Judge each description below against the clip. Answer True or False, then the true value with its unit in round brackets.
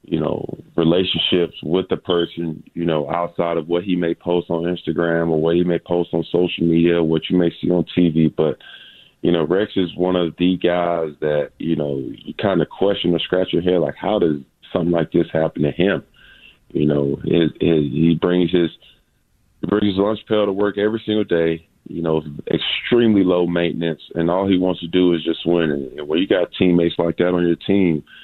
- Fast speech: True (210 wpm)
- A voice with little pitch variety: True (1.4 semitones)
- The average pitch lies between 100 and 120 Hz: False (85 Hz)